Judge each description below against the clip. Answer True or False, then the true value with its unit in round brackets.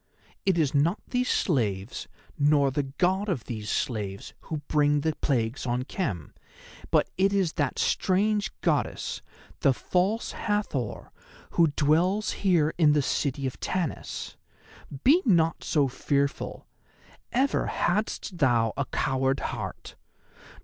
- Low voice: False (150 Hz)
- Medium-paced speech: False (125 wpm)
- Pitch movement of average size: False (5.9 semitones)